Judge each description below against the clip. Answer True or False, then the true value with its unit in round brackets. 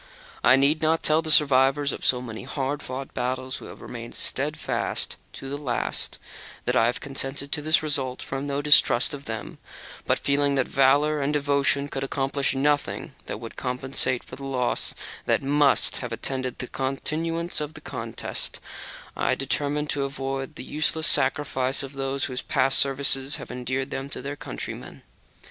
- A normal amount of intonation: False (1.6 semitones)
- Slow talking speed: False (175 wpm)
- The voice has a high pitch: False (135 Hz)